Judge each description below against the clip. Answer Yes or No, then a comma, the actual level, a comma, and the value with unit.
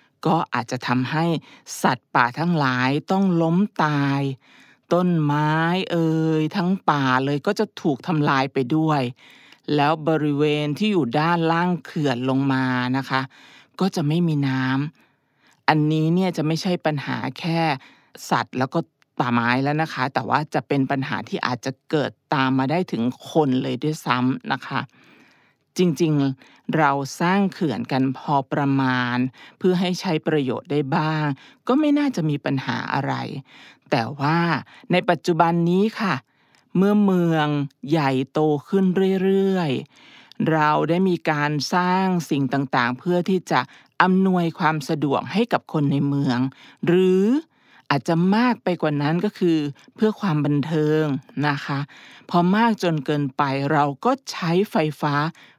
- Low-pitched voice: No, medium, 155 Hz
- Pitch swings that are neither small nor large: Yes, average, 4.4 semitones